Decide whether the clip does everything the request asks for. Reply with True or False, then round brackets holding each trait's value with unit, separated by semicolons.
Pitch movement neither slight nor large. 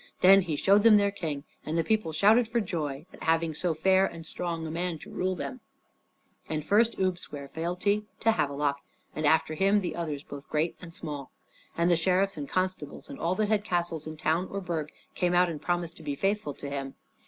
True (3.9 semitones)